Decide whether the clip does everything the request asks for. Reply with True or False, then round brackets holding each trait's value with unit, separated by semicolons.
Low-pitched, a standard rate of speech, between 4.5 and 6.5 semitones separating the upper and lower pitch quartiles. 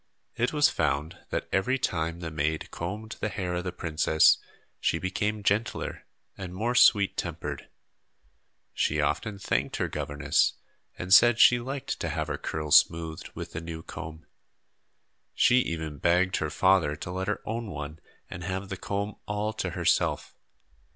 True (90 Hz; 160 wpm; 4.8 semitones)